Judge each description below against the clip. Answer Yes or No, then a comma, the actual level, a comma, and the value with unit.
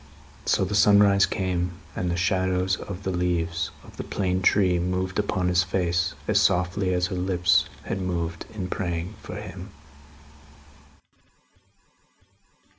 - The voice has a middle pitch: No, very low, 90 Hz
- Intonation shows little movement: Yes, narrow, 1.3 semitones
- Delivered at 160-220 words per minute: No, slow, 135 wpm